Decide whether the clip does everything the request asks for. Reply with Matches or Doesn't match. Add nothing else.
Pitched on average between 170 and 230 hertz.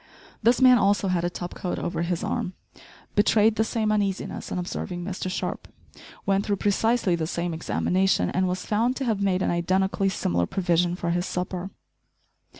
Matches